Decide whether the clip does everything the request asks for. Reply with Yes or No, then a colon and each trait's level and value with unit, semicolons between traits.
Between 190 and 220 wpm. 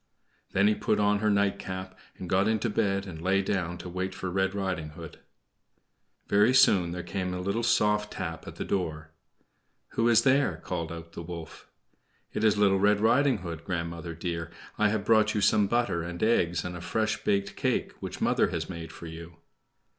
Yes: average, 195 wpm